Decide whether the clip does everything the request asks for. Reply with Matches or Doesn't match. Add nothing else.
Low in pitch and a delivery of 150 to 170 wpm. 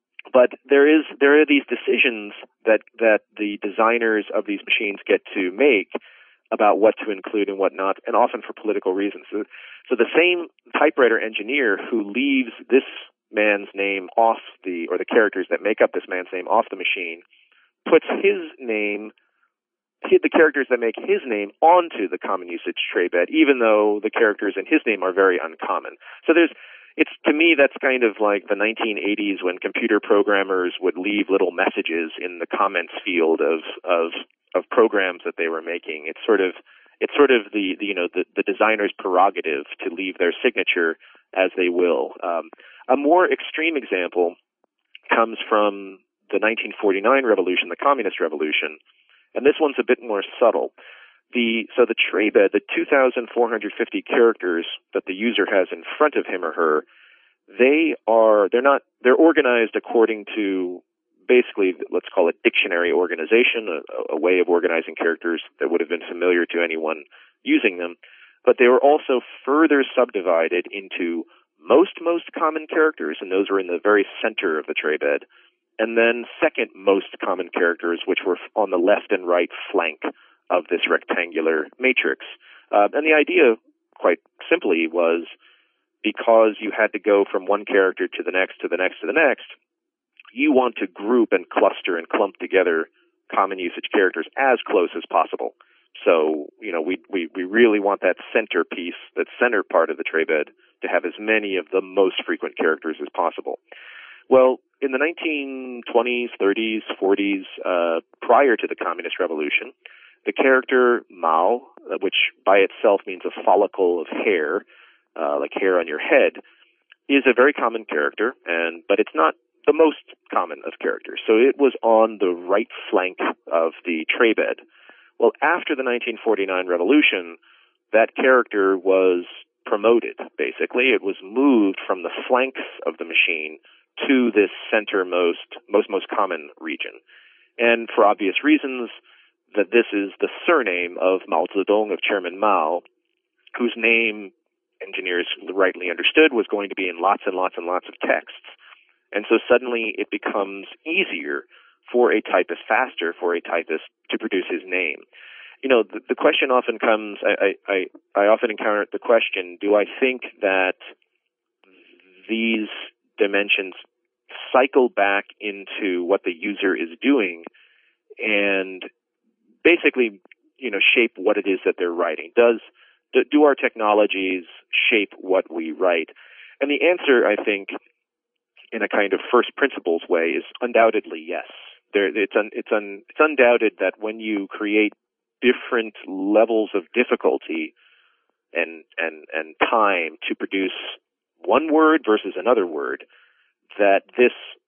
Matches